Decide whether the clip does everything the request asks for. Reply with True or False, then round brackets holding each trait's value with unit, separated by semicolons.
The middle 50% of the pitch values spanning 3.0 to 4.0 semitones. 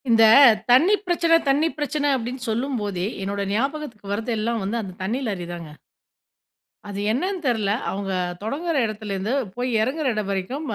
False (5.5 semitones)